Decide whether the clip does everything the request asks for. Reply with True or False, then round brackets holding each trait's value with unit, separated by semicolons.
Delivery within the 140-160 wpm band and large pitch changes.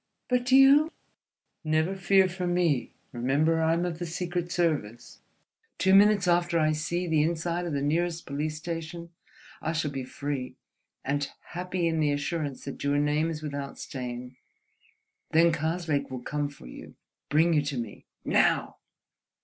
False (155 wpm; 3.4 semitones)